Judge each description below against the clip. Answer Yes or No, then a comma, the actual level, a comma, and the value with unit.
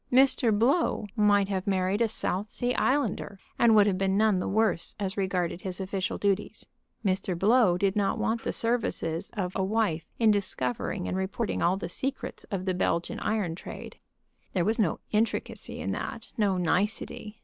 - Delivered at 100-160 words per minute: No, average, 175 wpm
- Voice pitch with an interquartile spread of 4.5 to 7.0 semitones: No, average, 2.8 semitones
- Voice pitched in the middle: No, high, 200 Hz